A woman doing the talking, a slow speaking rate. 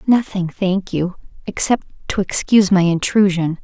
Yes: female; slow, 115 wpm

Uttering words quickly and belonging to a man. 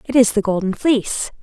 No: fast, 210 wpm; female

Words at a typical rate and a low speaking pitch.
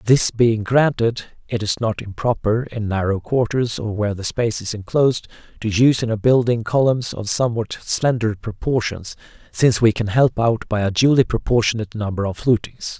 Yes: average, 175 wpm; low, 115 Hz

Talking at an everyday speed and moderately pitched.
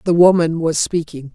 Yes: average, 180 wpm; medium, 165 Hz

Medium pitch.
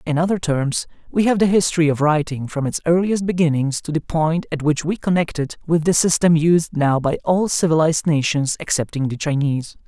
Yes: medium, 160 Hz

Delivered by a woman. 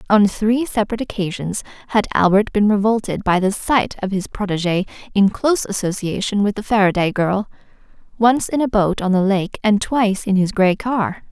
Yes: female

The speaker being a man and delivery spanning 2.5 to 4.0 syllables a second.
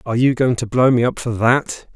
No: male; 5.6 syllables/s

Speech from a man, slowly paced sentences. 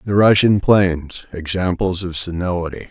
Yes: male; slow, 105 wpm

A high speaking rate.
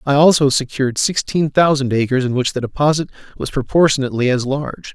No: average, 170 wpm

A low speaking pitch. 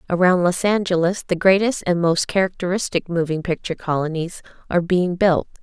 No: medium, 180 Hz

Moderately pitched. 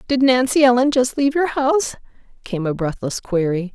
No: high, 235 Hz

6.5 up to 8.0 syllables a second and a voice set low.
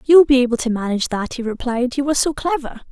No: 7.0 syllables/s; very high, 255 Hz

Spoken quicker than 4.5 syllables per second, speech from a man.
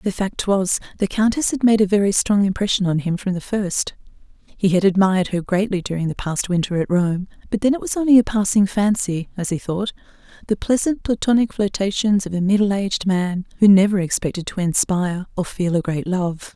No: 5.5 syllables/s; female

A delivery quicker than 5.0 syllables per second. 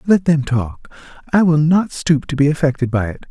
Yes: 5.2 syllables/s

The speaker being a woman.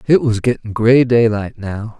No: male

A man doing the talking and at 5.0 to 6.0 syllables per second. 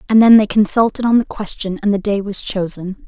No: female; 5.6 syllables/s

